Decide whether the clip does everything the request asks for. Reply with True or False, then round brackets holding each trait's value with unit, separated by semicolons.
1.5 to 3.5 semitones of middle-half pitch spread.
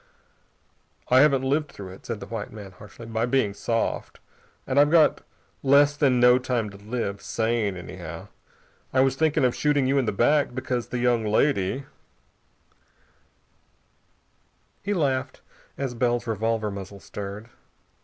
False (4.4 semitones)